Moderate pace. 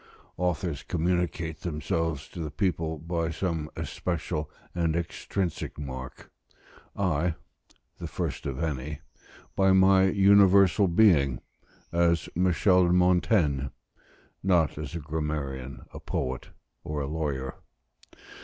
No: slow, 110 wpm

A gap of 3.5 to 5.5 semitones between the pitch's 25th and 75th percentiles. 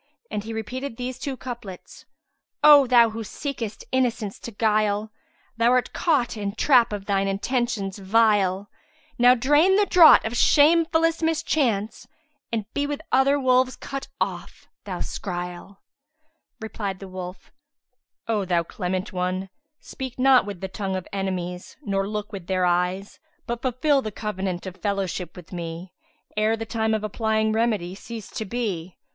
Yes: average, 4.7 semitones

